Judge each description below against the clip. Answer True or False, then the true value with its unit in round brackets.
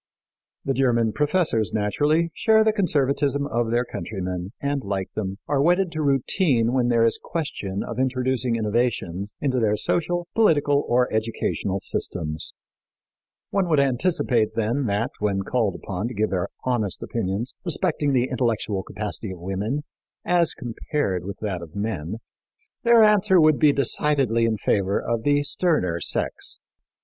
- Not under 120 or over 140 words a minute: False (150 wpm)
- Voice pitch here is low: True (120 Hz)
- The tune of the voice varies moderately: False (5.8 semitones)